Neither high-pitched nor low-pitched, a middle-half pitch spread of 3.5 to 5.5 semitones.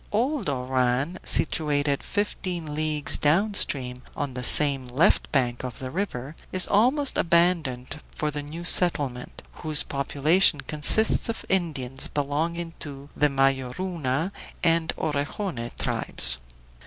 Yes: medium, 150 Hz; average, 4.5 semitones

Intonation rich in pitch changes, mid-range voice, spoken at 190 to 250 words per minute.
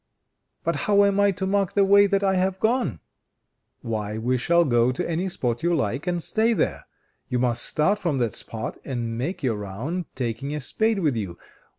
Yes: wide, 8.4 semitones; medium, 150 Hz; average, 200 wpm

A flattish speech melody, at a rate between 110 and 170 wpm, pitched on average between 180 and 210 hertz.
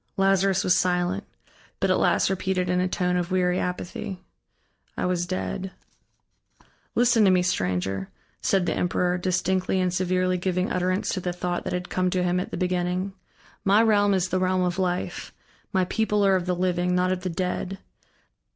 No: narrow, 0.9 semitones; average, 180 wpm; medium, 185 Hz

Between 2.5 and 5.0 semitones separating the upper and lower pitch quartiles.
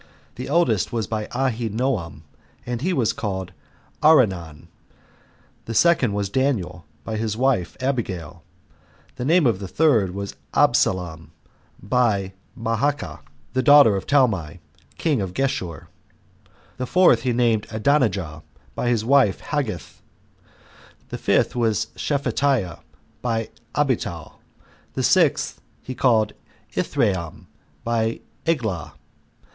No: wide, 5.5 semitones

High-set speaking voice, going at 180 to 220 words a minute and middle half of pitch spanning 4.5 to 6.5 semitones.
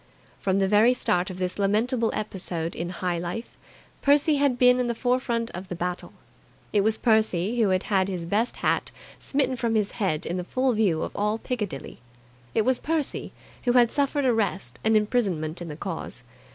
Yes: high, 210 Hz; average, 190 wpm; average, 5.2 semitones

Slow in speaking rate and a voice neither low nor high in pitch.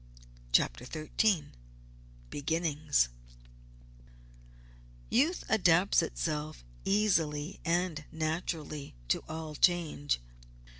Yes: slow, 65 wpm; medium, 160 Hz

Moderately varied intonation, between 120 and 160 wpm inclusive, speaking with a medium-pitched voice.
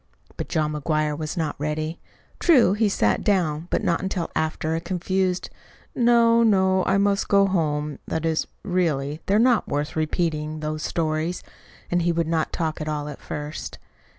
No: average, 3.6 semitones; average, 170 wpm; medium, 165 Hz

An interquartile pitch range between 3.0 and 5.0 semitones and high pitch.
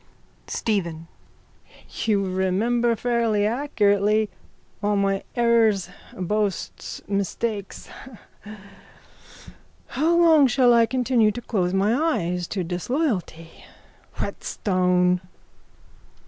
Yes: average, 4.1 semitones; high, 210 Hz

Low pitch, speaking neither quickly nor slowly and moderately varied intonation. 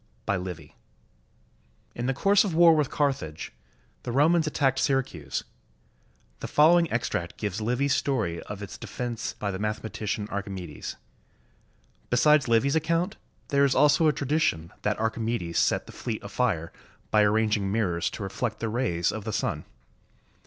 No: low, 115 Hz; average, 155 wpm; wide, 5.8 semitones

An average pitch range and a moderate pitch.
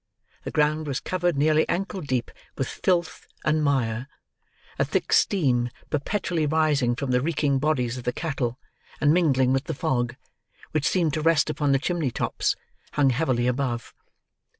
Yes: average, 3.8 semitones; medium, 145 Hz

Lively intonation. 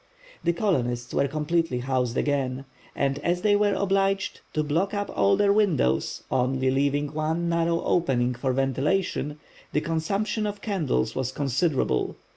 Yes: wide, 5.8 semitones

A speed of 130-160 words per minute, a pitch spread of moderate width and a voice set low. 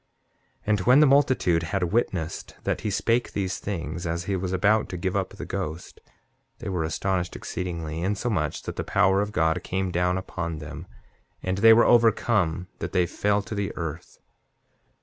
No: average, 180 wpm; average, 3.5 semitones; very low, 95 Hz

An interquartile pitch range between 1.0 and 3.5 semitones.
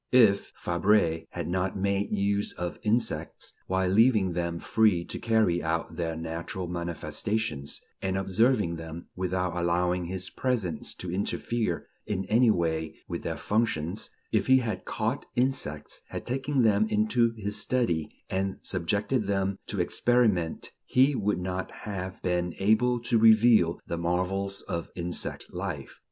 No: average, 4.1 semitones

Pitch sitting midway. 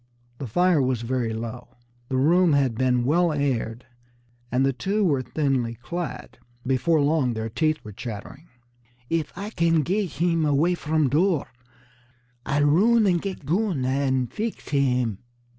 Yes: medium, 145 Hz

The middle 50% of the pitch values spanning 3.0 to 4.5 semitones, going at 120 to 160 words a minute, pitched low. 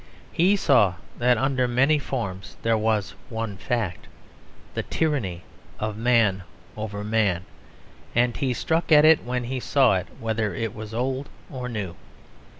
Yes: average, 3.8 semitones; average, 150 wpm; low, 115 Hz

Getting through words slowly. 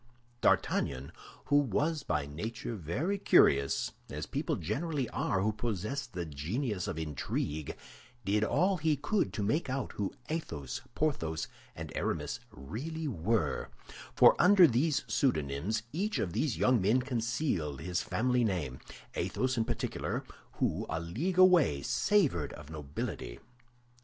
Yes: slow, 125 wpm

